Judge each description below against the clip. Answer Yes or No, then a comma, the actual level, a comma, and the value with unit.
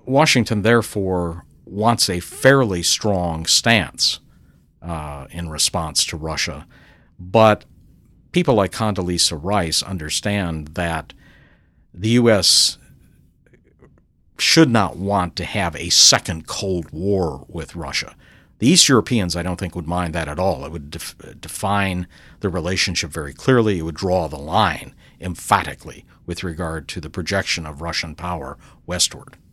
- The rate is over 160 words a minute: No, slow, 135 wpm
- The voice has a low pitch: Yes, very low, 90 Hz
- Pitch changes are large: No, average, 3.5 semitones